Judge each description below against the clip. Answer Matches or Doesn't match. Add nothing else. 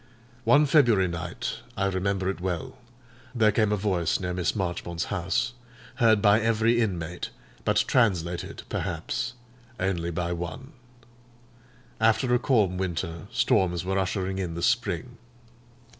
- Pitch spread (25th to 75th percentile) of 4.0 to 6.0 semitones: Matches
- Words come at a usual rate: Doesn't match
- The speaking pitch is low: Matches